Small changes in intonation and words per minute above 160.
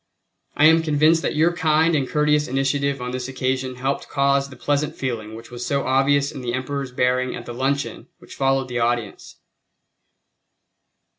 Yes: narrow, 2.3 semitones; average, 170 wpm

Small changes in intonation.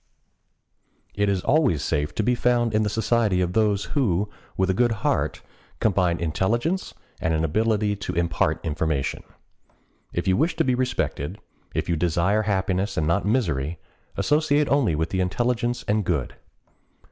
No: wide, 5.6 semitones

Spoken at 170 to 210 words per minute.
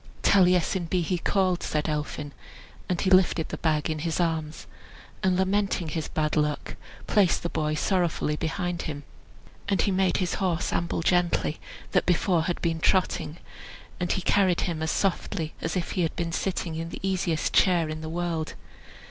Yes: average, 175 wpm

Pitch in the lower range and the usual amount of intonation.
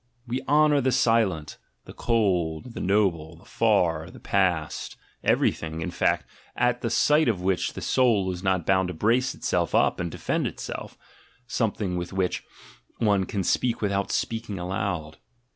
Yes: low, 100 Hz; average, 4.7 semitones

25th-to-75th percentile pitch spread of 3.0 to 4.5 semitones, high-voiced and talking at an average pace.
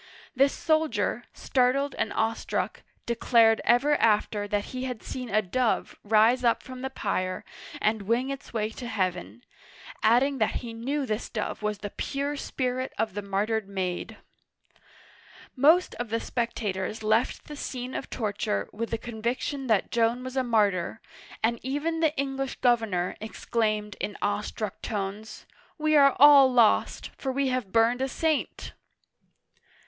Yes: average, 3.7 semitones; high, 235 Hz; average, 155 wpm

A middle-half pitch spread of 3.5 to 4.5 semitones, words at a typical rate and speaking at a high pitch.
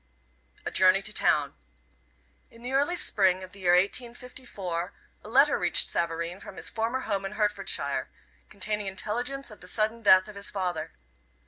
Yes: average, 4.1 semitones; average, 160 wpm; high, 205 Hz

